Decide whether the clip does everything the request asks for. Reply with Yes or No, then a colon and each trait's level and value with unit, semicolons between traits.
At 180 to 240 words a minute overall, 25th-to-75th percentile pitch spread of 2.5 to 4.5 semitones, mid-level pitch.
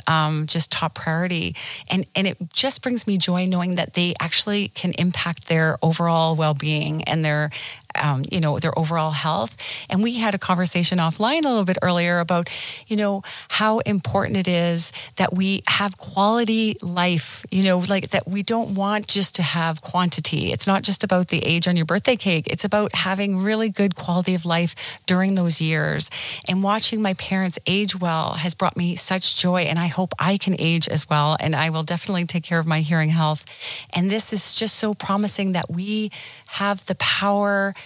Yes: average, 195 wpm; average, 3.5 semitones; medium, 180 Hz